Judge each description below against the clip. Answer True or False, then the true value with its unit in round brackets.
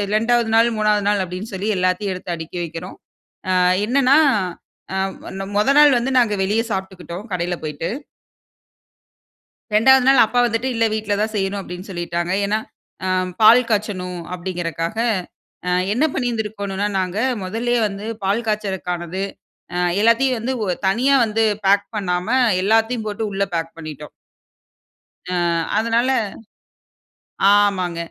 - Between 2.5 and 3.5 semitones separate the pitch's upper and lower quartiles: False (3.9 semitones)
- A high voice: True (205 Hz)